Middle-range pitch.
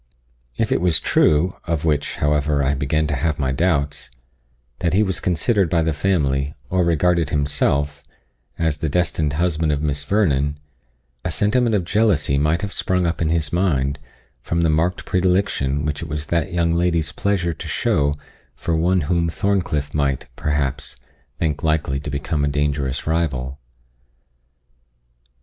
No: very low, 80 Hz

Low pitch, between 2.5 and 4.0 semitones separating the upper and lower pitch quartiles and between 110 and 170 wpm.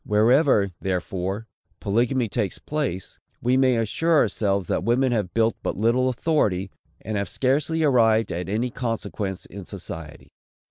No: low, 115 Hz; average, 4.5 semitones; slow, 135 wpm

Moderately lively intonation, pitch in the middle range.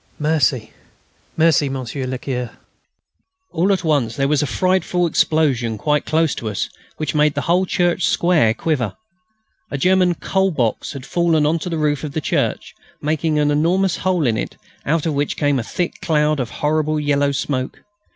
Yes: average, 3.3 semitones; medium, 150 Hz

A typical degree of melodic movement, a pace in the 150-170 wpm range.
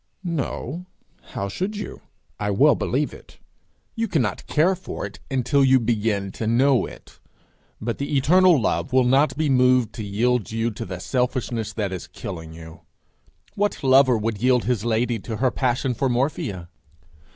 Yes: average, 4.0 semitones; average, 165 wpm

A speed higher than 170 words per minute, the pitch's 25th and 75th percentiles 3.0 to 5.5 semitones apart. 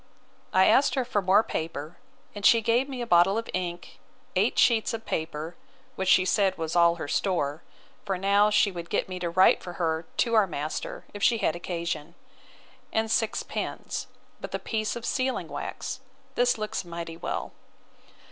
Yes: average, 180 wpm; average, 4.6 semitones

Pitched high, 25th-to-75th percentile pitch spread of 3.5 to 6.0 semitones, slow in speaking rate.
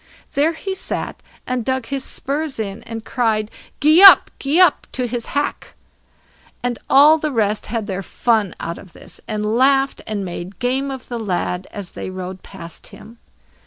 No: high, 235 Hz; average, 5.2 semitones; average, 175 wpm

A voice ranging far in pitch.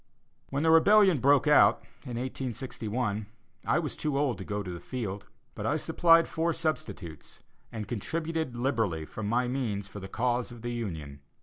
Yes: wide, 6.2 semitones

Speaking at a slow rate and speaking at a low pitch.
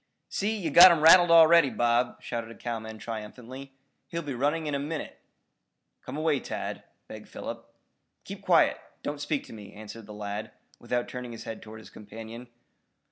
No: average, 175 wpm; low, 125 Hz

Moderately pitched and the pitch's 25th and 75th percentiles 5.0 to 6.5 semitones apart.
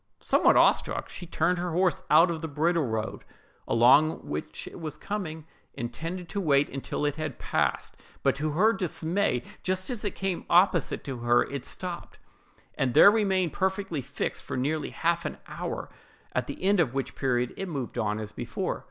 Yes: medium, 160 Hz; average, 5.3 semitones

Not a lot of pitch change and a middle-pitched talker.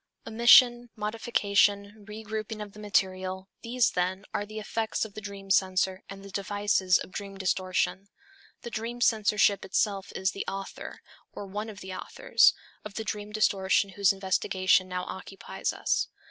No: narrow, 2.1 semitones; high, 200 Hz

